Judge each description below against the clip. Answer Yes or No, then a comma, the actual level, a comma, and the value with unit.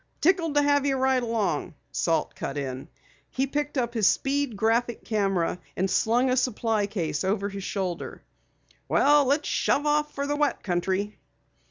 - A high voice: Yes, high, 230 Hz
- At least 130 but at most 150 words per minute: No, average, 165 wpm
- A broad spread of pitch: Yes, wide, 6.4 semitones